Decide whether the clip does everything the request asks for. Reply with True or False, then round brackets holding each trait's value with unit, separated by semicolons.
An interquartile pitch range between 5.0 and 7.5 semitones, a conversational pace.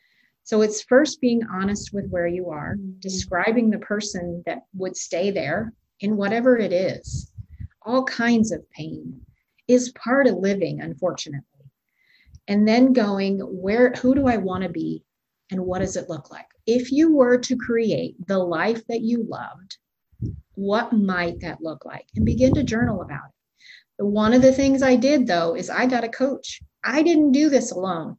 True (5.3 semitones; 175 wpm)